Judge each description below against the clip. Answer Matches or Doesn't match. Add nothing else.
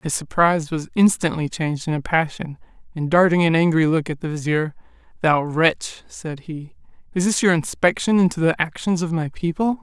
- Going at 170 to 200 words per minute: Matches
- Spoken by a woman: Doesn't match